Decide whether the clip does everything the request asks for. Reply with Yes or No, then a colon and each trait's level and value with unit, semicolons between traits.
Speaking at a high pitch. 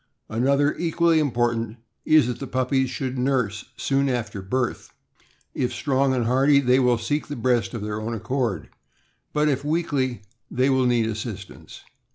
No: low, 130 Hz